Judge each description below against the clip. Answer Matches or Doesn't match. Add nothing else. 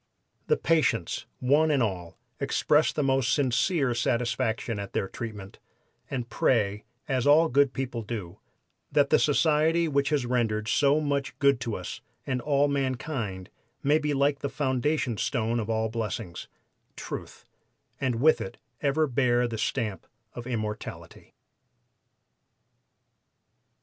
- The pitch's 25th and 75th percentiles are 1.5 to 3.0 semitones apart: Doesn't match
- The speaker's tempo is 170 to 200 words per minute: Doesn't match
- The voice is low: Matches